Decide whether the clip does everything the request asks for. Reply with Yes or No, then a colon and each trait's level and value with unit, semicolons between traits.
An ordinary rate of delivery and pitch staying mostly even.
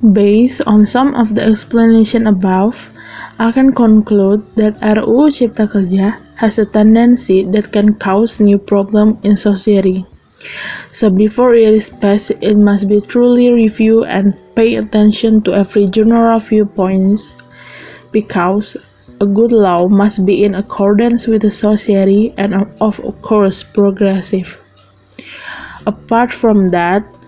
No: slow, 130 wpm; narrow, 2.1 semitones